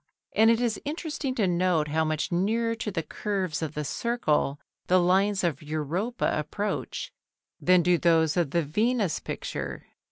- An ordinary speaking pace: Yes, average, 160 wpm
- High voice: No, medium, 180 Hz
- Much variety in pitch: Yes, wide, 5.7 semitones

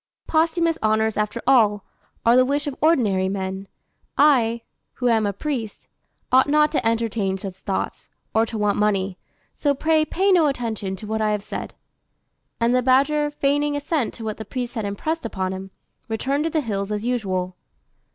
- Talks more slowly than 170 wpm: No, average, 180 wpm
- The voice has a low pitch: No, high, 230 Hz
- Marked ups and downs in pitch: Yes, wide, 5.7 semitones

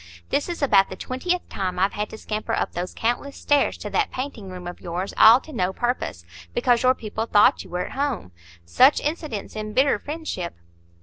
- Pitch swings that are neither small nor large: No, wide, 6.7 semitones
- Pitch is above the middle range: Yes, high, 225 Hz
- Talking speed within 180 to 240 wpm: Yes, average, 195 wpm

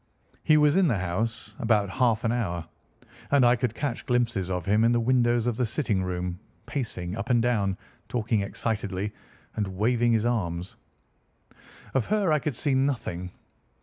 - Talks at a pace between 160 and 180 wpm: Yes, average, 170 wpm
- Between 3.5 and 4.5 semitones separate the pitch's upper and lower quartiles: Yes, average, 3.9 semitones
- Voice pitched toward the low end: Yes, low, 115 Hz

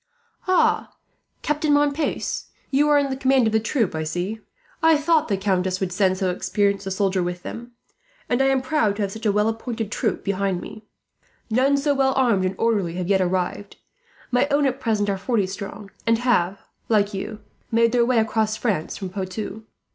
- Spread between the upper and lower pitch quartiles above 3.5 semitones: Yes, average, 5.0 semitones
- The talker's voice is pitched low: No, high, 215 Hz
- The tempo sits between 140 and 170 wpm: No, average, 195 wpm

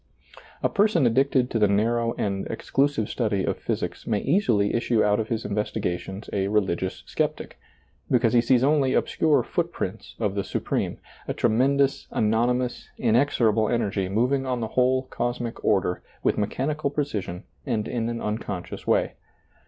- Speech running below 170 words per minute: Yes, average, 160 wpm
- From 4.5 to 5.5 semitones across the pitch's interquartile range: No, average, 3.7 semitones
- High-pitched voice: No, low, 115 Hz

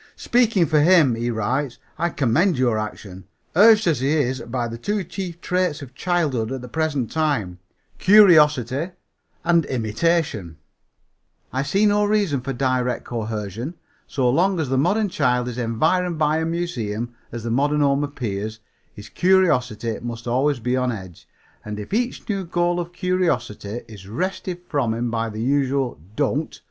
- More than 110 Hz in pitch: Yes, low, 135 Hz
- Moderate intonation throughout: No, wide, 6.6 semitones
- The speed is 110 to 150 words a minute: No, average, 160 wpm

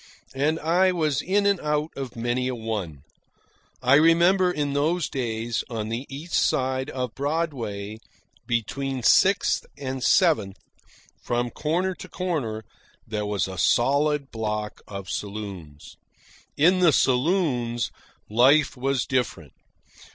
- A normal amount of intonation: No, wide, 5.7 semitones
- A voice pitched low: Yes, low, 130 Hz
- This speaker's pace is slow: Yes, slow, 125 wpm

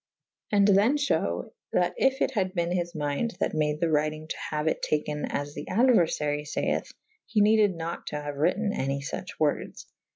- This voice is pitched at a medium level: Yes, medium, 165 Hz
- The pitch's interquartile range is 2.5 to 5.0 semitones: No, wide, 5.4 semitones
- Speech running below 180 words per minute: No, average, 190 wpm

